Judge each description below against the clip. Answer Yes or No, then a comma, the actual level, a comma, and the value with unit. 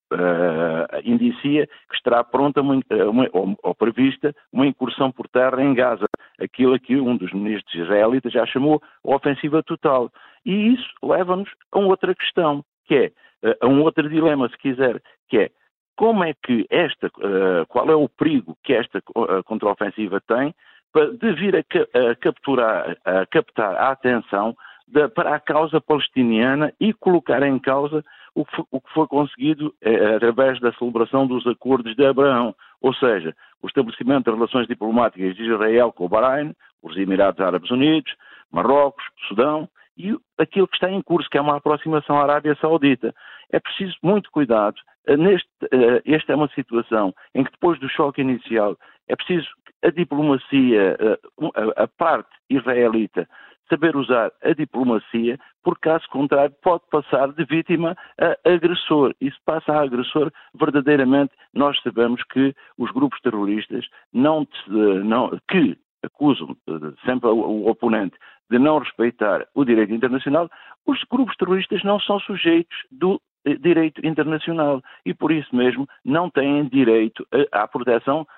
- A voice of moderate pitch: Yes, medium, 145 Hz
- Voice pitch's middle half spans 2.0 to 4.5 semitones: No, average, 4.9 semitones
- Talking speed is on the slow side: No, average, 150 wpm